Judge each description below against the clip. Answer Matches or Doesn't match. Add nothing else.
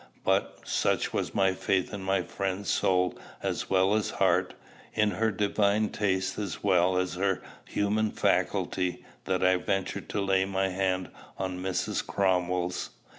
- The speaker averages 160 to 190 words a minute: Doesn't match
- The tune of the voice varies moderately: Doesn't match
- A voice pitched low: Matches